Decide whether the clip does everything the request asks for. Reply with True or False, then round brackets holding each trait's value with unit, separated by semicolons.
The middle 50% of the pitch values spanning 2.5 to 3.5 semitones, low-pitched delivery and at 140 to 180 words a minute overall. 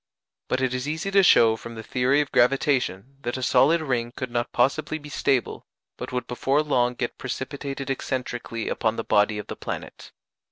False (2.8 semitones; 130 Hz; 190 wpm)